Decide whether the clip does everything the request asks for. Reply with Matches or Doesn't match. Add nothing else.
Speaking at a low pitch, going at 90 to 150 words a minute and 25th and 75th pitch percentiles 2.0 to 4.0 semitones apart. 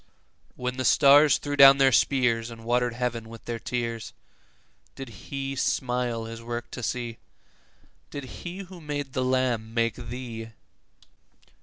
Matches